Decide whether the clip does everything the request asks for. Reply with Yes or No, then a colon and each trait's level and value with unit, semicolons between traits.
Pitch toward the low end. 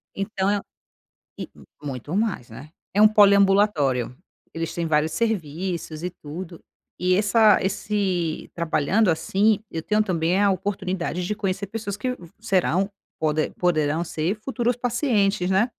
No: high, 190 Hz